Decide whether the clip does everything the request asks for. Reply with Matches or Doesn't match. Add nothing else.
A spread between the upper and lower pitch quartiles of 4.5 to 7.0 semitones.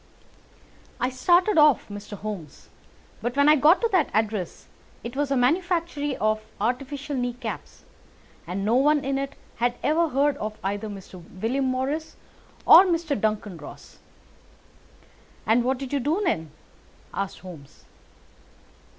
Matches